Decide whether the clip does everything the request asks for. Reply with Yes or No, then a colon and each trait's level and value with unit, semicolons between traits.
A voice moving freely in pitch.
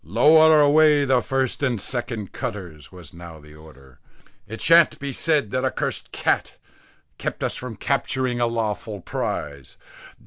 Yes: wide, 8.1 semitones